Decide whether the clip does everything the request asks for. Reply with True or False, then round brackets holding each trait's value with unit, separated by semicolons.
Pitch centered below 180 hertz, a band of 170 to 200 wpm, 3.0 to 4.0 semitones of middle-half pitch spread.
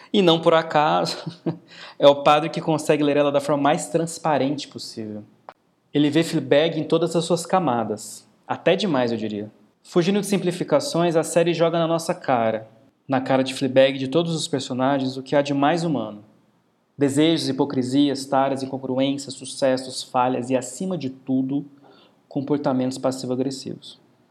False (140 Hz; 155 wpm; 3.7 semitones)